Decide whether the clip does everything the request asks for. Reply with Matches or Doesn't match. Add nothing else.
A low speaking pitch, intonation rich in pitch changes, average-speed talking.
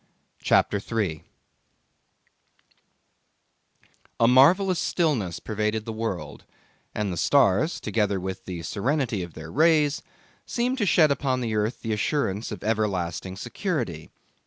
Doesn't match